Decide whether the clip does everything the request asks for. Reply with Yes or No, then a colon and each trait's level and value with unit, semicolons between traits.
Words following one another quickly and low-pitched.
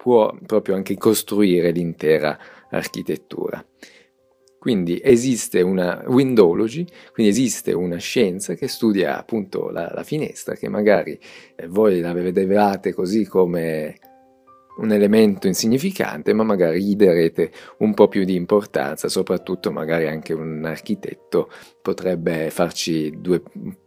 No: average, 120 wpm; low, 100 Hz